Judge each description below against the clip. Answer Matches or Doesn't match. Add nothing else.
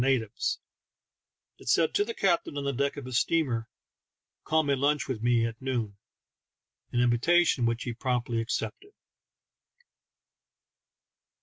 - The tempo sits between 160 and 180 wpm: Doesn't match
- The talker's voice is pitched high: Doesn't match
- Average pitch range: Matches